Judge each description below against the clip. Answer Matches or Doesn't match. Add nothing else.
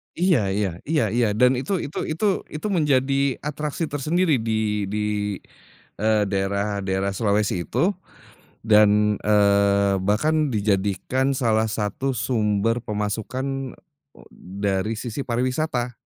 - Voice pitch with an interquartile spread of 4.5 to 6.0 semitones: Matches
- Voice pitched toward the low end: Matches